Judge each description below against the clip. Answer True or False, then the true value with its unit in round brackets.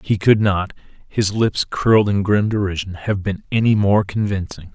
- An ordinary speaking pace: True (150 wpm)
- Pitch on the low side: True (100 Hz)